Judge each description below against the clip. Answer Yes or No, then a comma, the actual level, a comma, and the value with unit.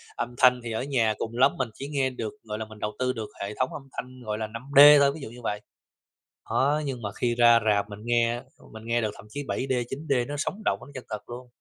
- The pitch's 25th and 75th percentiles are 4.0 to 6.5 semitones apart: No, average, 3.4 semitones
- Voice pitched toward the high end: No, low, 120 Hz